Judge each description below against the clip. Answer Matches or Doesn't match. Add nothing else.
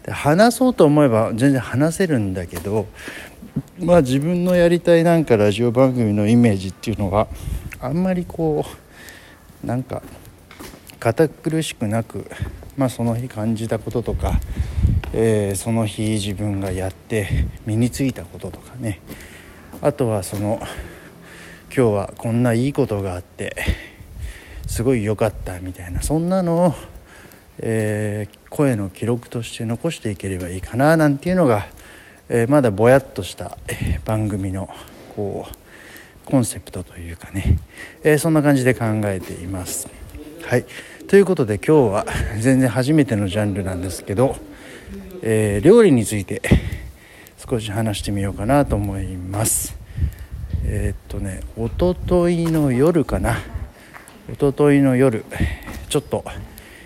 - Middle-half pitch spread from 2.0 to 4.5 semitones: Doesn't match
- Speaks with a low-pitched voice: Matches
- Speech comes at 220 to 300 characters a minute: Matches